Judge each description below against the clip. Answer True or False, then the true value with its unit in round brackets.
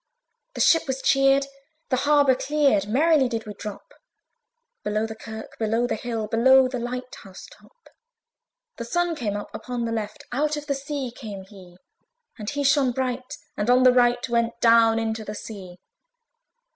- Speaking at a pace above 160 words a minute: True (170 wpm)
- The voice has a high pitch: True (245 Hz)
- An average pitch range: True (3.7 semitones)